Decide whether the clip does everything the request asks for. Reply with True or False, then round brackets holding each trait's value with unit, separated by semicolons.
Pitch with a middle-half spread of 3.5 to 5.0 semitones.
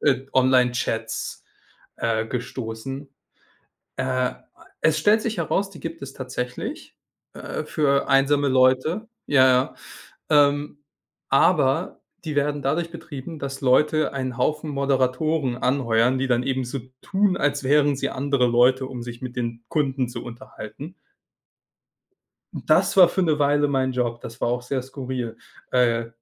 False (2.7 semitones)